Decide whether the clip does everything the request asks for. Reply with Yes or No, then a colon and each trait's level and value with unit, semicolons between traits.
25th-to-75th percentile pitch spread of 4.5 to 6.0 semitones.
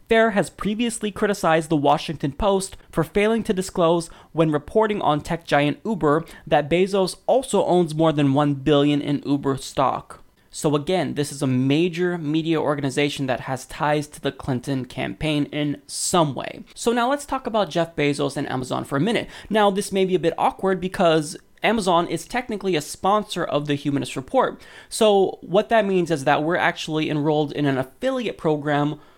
Yes: average, 5.1 semitones